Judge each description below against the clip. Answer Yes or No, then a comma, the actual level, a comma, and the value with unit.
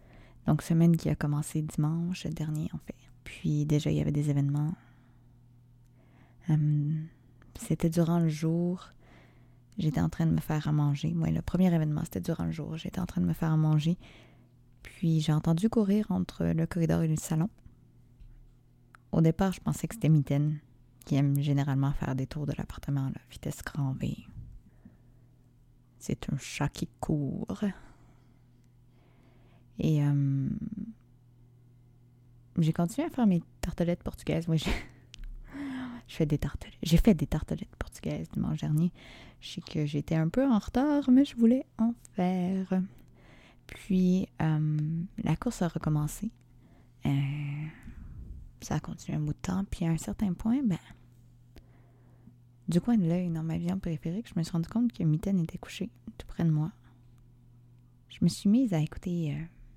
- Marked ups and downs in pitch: Yes, wide, 5.8 semitones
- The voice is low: No, medium, 150 Hz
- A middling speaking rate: Yes, average, 160 wpm